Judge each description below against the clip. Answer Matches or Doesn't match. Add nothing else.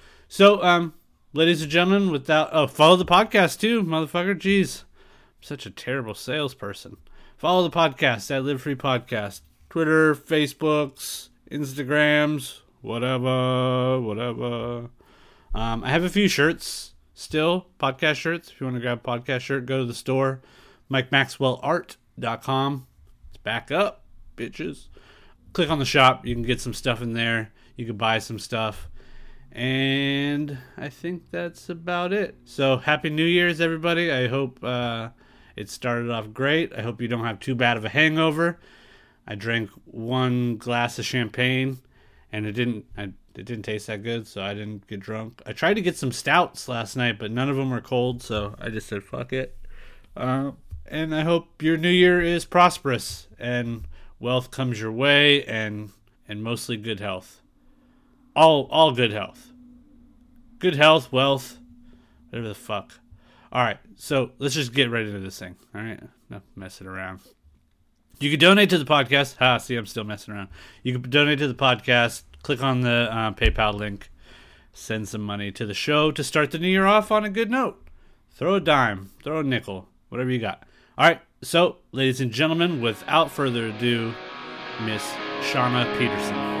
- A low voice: Matches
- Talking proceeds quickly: Doesn't match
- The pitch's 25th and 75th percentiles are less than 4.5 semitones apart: Doesn't match